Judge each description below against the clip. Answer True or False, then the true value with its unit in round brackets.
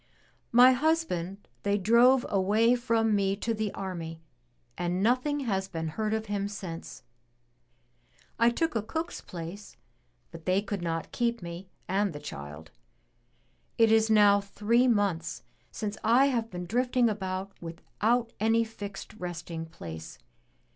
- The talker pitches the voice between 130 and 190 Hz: False (205 Hz)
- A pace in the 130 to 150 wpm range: True (140 wpm)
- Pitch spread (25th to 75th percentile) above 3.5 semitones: True (4.5 semitones)